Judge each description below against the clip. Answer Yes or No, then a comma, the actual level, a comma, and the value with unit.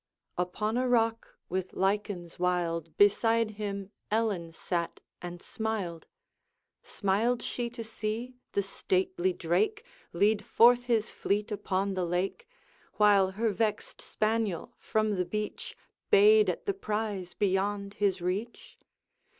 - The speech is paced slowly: Yes, slow, 125 wpm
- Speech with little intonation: No, average, 3.4 semitones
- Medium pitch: No, high, 210 Hz